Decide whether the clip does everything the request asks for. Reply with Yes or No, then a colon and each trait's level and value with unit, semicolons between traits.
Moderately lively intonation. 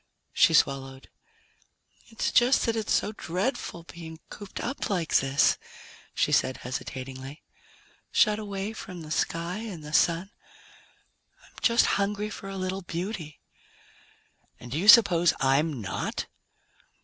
No: wide, 5.7 semitones